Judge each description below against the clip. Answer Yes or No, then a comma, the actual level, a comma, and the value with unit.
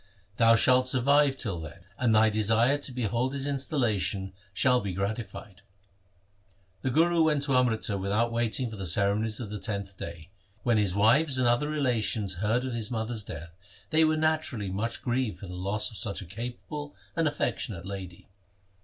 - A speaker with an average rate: Yes, average, 180 wpm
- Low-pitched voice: Yes, low, 115 Hz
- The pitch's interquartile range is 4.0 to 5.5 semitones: Yes, average, 4.6 semitones